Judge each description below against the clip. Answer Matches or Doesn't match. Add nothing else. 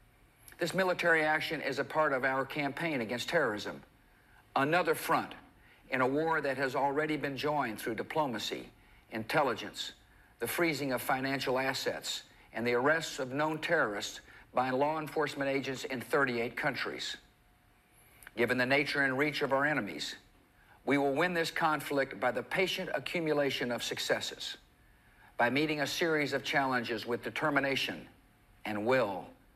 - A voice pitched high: Doesn't match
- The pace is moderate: Matches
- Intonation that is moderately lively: Matches